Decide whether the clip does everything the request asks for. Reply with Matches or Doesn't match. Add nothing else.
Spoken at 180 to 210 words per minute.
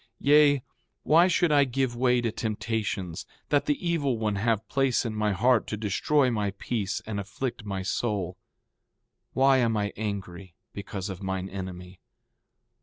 Doesn't match